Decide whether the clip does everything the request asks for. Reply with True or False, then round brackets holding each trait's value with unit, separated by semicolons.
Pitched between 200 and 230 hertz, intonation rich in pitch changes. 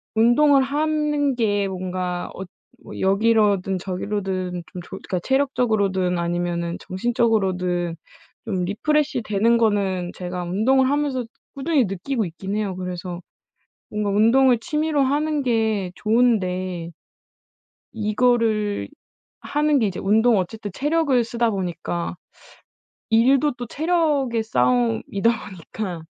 True (215 Hz; 5.7 semitones)